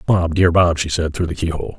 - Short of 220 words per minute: No, fast, 270 wpm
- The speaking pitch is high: No, very low, 85 Hz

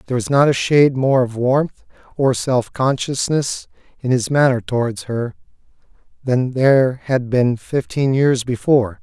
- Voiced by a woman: No, male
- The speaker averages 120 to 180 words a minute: Yes, average, 155 wpm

